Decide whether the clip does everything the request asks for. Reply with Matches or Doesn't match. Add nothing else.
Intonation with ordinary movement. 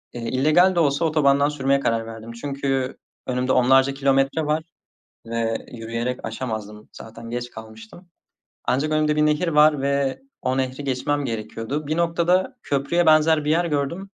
Matches